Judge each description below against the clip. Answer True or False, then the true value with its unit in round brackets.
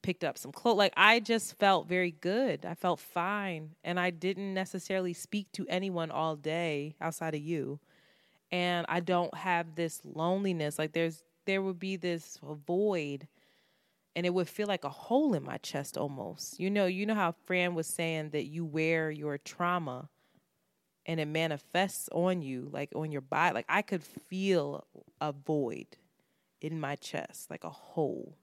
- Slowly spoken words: False (175 wpm)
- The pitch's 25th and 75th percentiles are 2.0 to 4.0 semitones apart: True (3.1 semitones)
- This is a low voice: False (170 Hz)